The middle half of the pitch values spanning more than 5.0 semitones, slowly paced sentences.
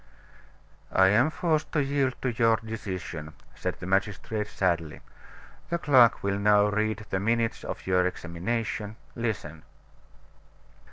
No: average, 3.8 semitones; slow, 125 wpm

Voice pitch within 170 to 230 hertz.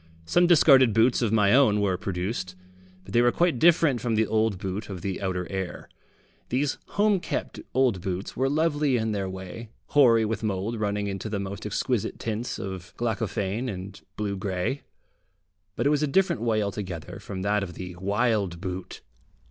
No: low, 105 Hz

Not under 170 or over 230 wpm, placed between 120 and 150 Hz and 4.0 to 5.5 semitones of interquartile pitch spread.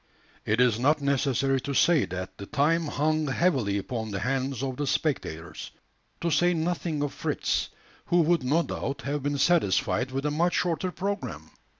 Yes: average, 175 wpm; medium, 140 Hz; average, 4.5 semitones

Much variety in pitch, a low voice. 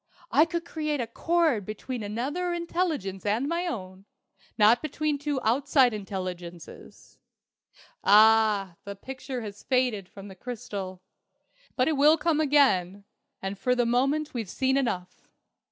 No: wide, 6.6 semitones; high, 245 Hz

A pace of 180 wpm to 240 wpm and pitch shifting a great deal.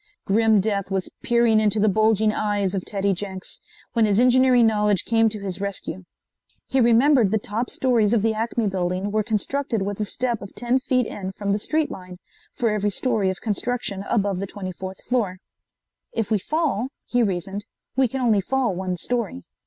No: average, 185 wpm; average, 3.3 semitones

